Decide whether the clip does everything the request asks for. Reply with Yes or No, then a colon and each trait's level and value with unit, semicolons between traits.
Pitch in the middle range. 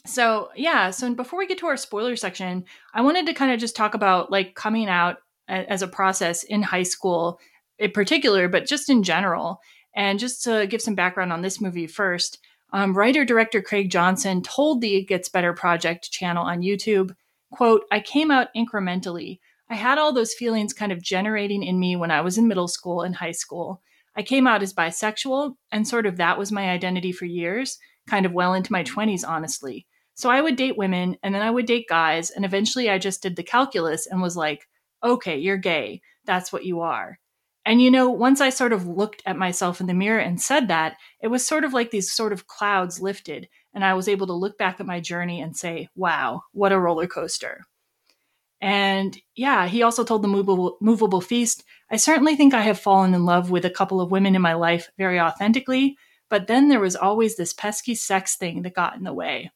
No: high, 195 Hz